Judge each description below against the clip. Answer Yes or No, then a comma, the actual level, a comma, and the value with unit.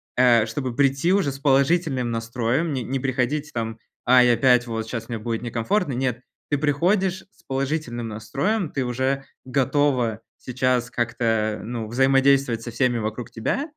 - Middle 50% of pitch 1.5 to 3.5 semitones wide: Yes, average, 3.1 semitones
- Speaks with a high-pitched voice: No, low, 125 Hz